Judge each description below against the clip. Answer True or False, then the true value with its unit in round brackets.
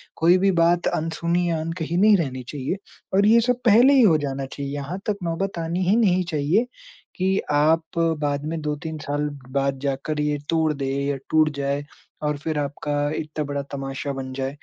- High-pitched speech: False (155 Hz)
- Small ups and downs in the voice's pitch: False (3.7 semitones)